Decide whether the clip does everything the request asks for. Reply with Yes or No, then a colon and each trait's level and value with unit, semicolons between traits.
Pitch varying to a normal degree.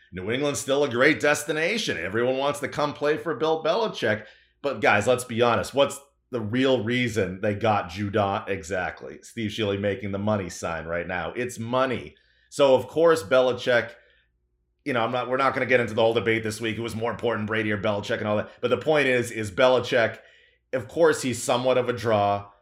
Yes: average, 3.9 semitones